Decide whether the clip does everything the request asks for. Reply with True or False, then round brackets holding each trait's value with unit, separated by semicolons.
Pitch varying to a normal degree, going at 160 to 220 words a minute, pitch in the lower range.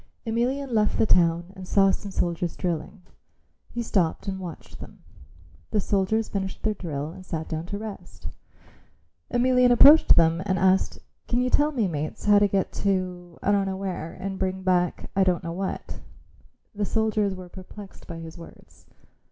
False (3.1 semitones; 175 wpm; 190 Hz)